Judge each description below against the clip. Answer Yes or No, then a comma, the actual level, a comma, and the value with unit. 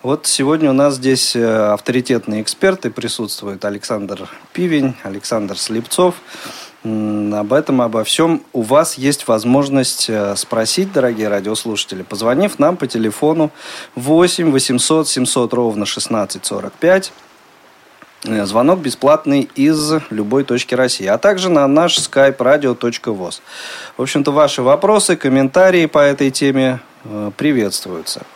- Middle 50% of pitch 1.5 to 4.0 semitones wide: No, wide, 5.6 semitones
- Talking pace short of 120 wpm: Yes, slow, 110 wpm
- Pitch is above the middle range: No, low, 130 Hz